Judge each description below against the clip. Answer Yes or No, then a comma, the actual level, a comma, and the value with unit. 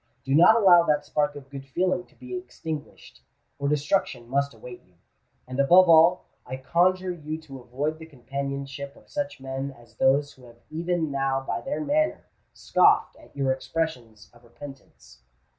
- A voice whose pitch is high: No, medium, 140 Hz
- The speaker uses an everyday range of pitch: Yes, average, 4.1 semitones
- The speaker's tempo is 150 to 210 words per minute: Yes, average, 165 wpm